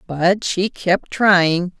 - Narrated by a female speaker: Yes, female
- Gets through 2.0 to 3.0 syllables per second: Yes, 2.5 syllables/s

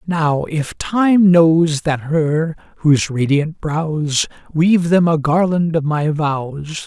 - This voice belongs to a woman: No, male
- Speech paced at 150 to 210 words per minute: No, average, 140 wpm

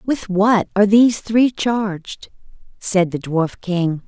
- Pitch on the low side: No, high, 200 Hz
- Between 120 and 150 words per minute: Yes, average, 145 wpm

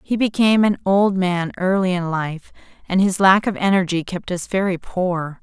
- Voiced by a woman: Yes, female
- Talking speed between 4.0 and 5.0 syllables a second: Yes, 4.7 syllables/s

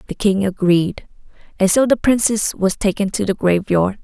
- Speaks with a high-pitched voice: Yes, high, 200 Hz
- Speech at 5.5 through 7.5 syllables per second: No, 4.8 syllables/s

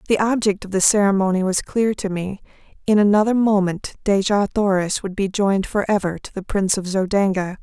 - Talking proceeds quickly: No, average, 180 wpm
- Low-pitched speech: No, high, 200 Hz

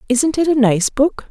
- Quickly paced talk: Yes, fast, 230 wpm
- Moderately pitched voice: No, very high, 265 Hz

